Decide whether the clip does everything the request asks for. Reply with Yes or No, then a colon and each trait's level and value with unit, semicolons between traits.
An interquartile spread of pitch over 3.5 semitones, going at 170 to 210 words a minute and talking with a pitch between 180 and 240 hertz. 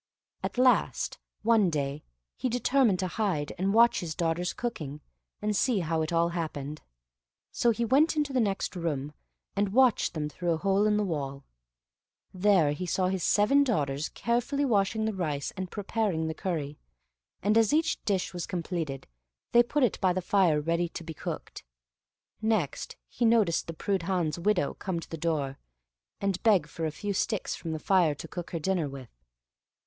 Yes: average, 5.1 semitones; average, 180 wpm; medium, 185 Hz